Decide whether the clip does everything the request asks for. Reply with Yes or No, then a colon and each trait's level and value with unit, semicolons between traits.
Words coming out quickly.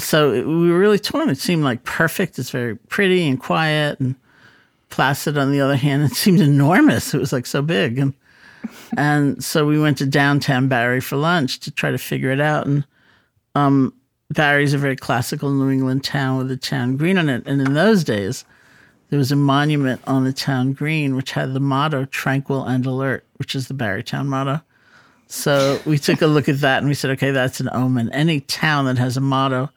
Yes: fast, 210 wpm